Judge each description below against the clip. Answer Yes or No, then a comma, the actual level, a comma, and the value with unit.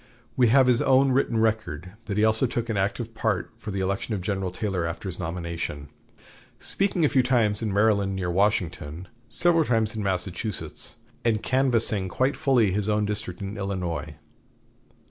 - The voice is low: Yes, low, 105 Hz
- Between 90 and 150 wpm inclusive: No, average, 170 wpm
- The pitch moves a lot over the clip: No, average, 3.9 semitones